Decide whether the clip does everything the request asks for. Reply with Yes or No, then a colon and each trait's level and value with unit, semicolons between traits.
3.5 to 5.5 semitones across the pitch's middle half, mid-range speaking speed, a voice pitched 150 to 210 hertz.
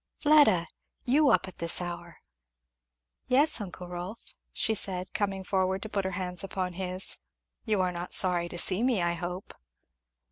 No: average, 2.7 semitones; average, 165 wpm; medium, 185 Hz